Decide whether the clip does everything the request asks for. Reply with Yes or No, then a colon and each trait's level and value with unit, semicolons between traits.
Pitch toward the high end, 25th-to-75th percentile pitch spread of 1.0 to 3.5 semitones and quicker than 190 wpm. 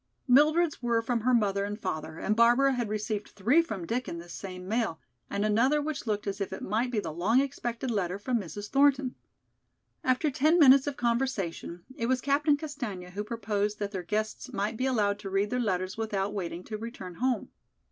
No: high, 220 Hz; average, 4.4 semitones; average, 200 wpm